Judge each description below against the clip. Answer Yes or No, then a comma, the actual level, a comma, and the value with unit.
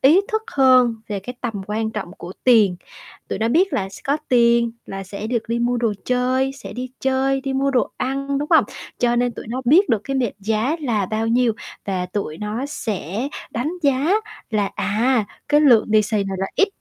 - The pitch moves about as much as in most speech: Yes, average, 3.9 semitones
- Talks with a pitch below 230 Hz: No, high, 240 Hz